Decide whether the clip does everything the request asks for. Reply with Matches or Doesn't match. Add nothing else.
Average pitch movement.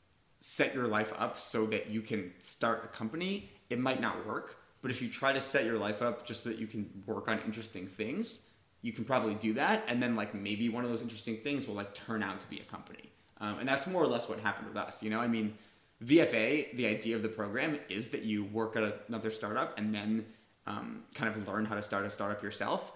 Doesn't match